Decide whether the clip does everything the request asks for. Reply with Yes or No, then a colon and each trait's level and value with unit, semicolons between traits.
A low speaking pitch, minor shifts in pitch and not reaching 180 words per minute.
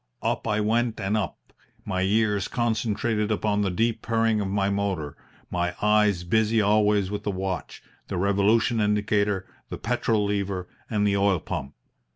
Yes: low, 105 Hz; narrow, 1.9 semitones; average, 160 wpm